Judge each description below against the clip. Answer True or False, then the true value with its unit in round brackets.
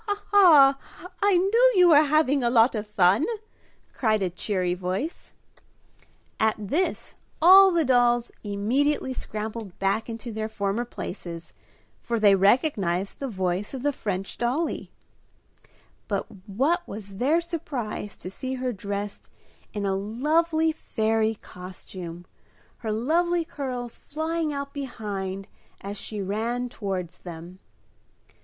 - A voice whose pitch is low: False (230 Hz)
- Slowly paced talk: True (130 wpm)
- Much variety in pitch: True (6.6 semitones)